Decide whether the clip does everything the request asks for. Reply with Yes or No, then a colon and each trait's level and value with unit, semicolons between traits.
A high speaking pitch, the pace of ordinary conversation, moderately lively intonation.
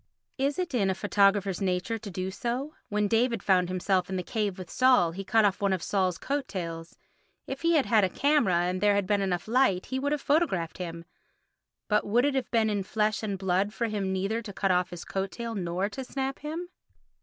No: high, 205 Hz; fast, 220 wpm; average, 4.7 semitones